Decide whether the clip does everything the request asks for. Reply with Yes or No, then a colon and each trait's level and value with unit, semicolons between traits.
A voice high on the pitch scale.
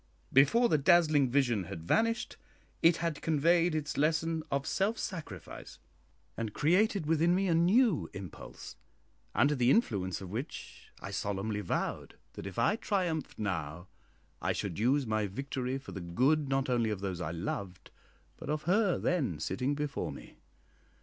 No: medium, 140 Hz